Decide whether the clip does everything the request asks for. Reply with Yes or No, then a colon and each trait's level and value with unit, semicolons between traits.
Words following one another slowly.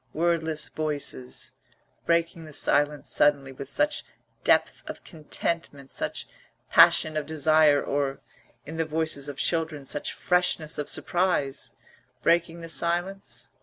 Yes: slow, 125 wpm